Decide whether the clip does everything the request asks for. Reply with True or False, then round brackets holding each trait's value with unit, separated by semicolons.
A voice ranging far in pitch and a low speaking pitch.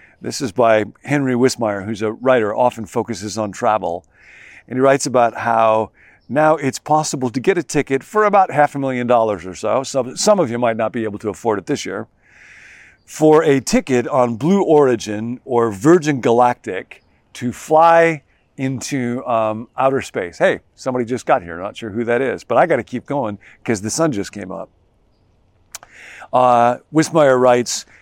False (4.2 semitones; 125 Hz)